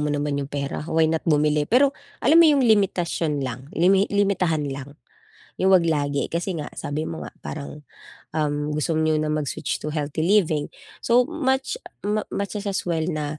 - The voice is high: No, medium, 160 Hz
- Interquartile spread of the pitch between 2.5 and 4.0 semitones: No, average, 5.1 semitones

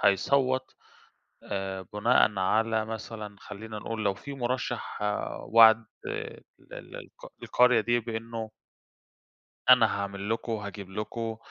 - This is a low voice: Yes, low, 110 Hz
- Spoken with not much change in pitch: Yes, narrow, 2.1 semitones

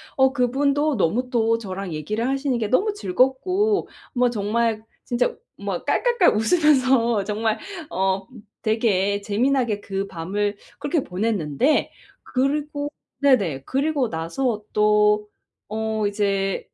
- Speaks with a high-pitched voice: Yes, high, 230 Hz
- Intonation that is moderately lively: Yes, average, 5.0 semitones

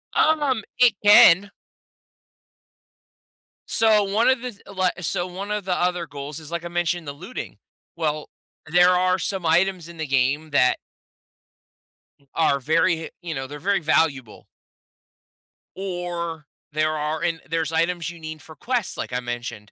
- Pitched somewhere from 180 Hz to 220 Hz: No, medium, 170 Hz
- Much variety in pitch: No, average, 3.5 semitones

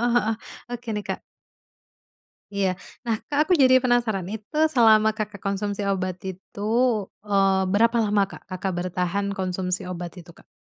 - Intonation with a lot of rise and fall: No, average, 3.1 semitones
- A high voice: Yes, high, 200 Hz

